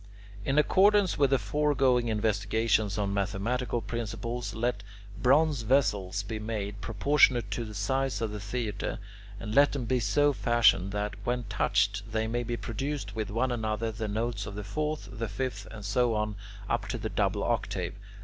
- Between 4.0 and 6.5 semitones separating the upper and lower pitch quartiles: No, average, 3.4 semitones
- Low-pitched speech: Yes, low, 115 Hz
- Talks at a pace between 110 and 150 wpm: No, average, 170 wpm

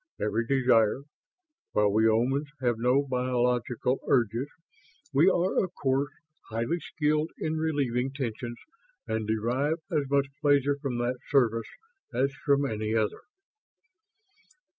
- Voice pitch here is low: Yes, low, 130 Hz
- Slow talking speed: Yes, slow, 120 wpm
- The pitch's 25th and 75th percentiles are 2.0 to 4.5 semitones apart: Yes, average, 3.5 semitones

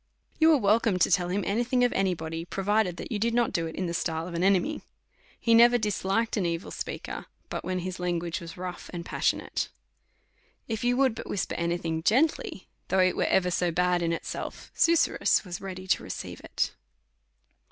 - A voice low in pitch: No, medium, 185 Hz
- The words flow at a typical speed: No, fast, 210 wpm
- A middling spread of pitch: Yes, average, 4.3 semitones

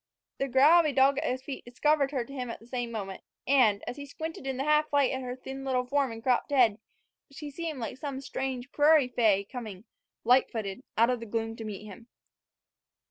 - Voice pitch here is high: Yes, very high, 255 Hz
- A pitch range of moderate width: Yes, average, 3.3 semitones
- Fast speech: Yes, fast, 225 wpm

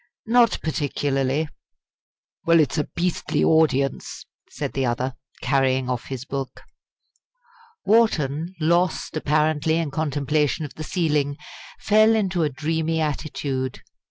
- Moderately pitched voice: Yes, medium, 150 Hz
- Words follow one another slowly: Yes, slow, 115 wpm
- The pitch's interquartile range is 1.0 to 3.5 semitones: Yes, average, 3.1 semitones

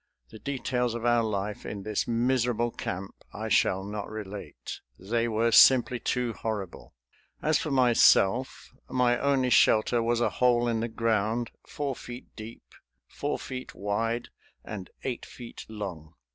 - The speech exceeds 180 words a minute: No, average, 145 wpm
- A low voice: Yes, low, 115 Hz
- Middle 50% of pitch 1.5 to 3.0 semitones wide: Yes, average, 2.7 semitones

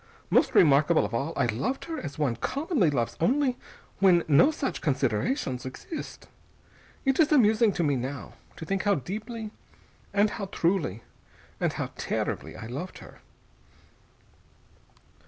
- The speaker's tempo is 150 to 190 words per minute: No, average, 140 wpm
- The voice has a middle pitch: Yes, medium, 175 Hz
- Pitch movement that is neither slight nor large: No, wide, 8.8 semitones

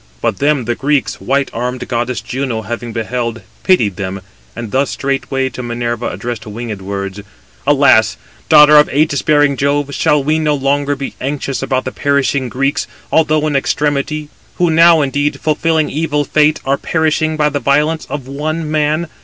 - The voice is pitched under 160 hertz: Yes, medium, 140 Hz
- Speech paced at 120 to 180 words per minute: Yes, average, 160 wpm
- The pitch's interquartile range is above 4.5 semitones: No, average, 3.3 semitones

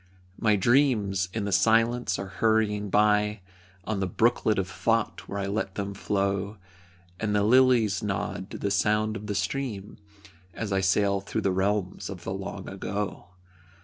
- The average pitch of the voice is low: Yes, low, 105 Hz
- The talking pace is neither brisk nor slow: Yes, average, 165 wpm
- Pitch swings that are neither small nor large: No, narrow, 1.9 semitones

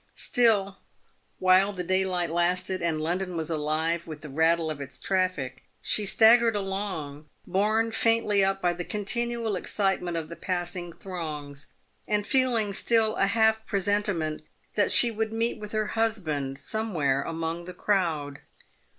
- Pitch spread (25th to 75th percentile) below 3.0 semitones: No, average, 4.6 semitones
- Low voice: No, medium, 185 Hz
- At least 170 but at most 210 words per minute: No, average, 145 wpm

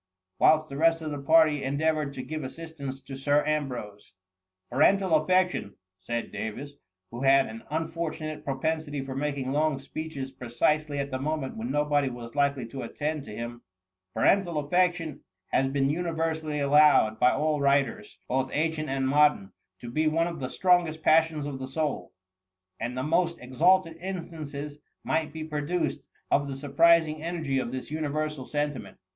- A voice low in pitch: No, medium, 150 Hz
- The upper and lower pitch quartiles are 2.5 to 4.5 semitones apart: Yes, average, 2.9 semitones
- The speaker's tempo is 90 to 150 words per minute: No, average, 170 wpm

